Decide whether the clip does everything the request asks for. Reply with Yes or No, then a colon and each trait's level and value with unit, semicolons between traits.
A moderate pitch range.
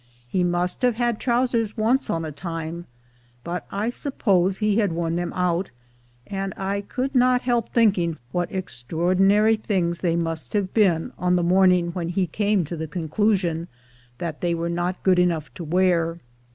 Yes: average, 3.5 semitones